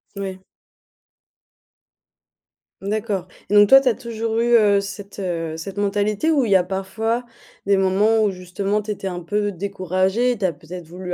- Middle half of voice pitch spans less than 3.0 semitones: Yes, narrow, 2.5 semitones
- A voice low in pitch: No, high, 200 Hz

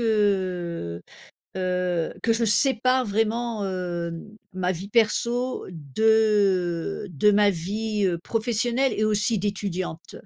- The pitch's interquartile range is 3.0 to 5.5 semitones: Yes, average, 3.8 semitones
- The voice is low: No, high, 205 Hz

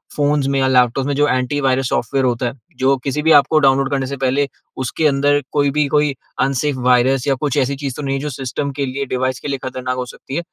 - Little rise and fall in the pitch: Yes, narrow, 1.8 semitones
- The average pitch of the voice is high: No, low, 135 Hz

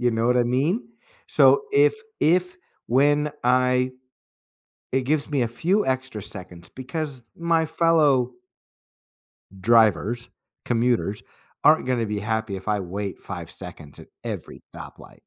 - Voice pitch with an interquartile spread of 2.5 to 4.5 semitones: No, average, 5.1 semitones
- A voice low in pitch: Yes, low, 125 Hz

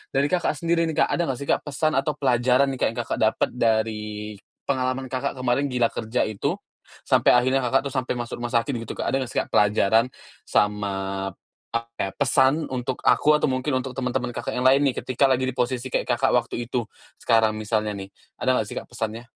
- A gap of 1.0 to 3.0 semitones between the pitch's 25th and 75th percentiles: Yes, average, 2.7 semitones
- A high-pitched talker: No, low, 125 Hz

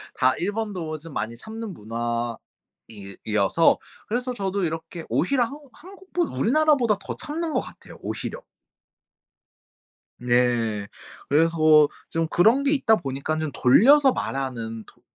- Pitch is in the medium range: Yes, medium, 165 Hz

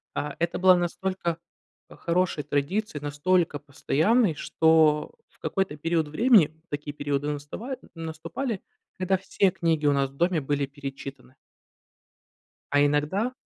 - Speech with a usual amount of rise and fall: Yes, average, 4.2 semitones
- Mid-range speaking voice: Yes, medium, 160 Hz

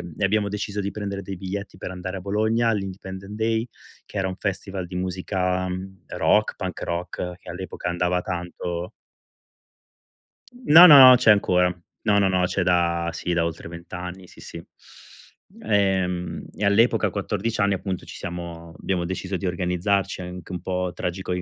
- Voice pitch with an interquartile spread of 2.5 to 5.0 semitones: No, narrow, 2.1 semitones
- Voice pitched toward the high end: No, very low, 95 Hz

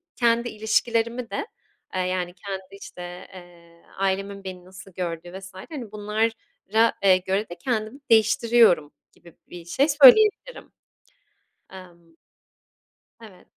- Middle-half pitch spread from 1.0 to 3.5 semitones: No, average, 4.1 semitones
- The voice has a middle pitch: No, high, 195 Hz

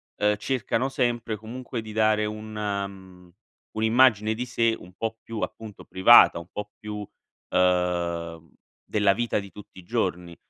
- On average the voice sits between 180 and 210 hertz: No, low, 105 Hz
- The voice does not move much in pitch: No, average, 3.4 semitones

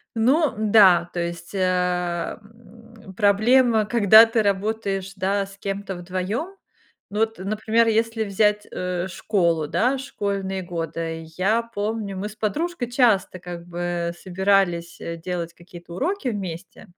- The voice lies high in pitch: Yes, high, 200 Hz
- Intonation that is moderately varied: Yes, average, 3.8 semitones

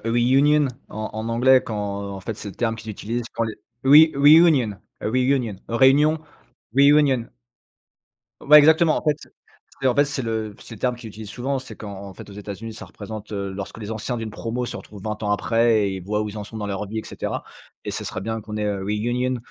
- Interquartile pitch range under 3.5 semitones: No, average, 3.9 semitones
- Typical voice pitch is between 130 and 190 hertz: No, low, 115 Hz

